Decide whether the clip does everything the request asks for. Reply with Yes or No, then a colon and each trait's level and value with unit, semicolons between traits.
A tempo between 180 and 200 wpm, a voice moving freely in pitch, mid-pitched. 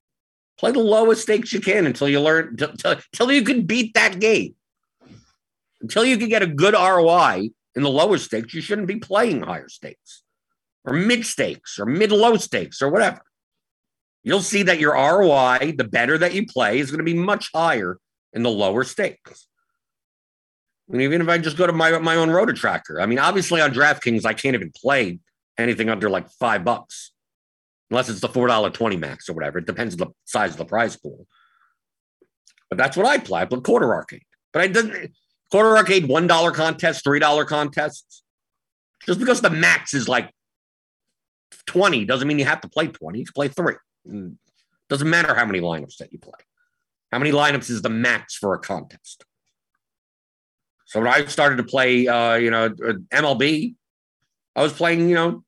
Yes: average, 190 wpm; wide, 8.0 semitones; medium, 160 Hz